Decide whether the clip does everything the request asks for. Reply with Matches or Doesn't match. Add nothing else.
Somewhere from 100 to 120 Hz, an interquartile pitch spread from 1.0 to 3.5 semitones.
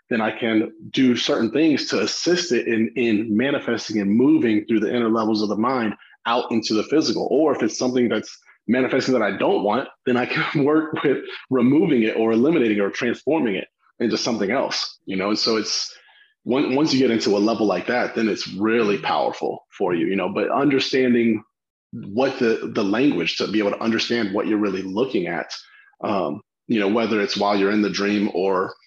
Matches